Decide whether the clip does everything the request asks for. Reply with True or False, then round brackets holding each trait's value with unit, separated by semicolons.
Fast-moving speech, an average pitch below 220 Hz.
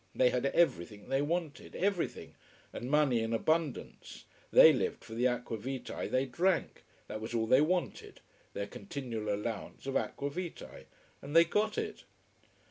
False (155 wpm; 135 Hz)